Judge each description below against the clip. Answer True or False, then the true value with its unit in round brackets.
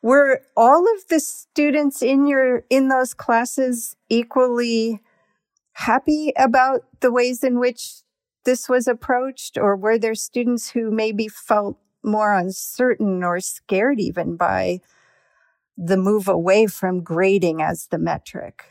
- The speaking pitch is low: False (240 Hz)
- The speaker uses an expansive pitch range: False (4.0 semitones)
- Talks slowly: True (130 wpm)